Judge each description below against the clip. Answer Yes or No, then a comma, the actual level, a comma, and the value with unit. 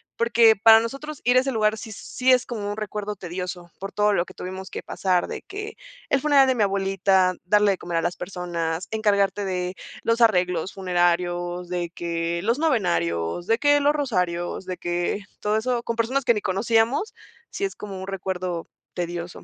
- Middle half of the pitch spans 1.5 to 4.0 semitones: No, average, 4.5 semitones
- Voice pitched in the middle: No, high, 195 Hz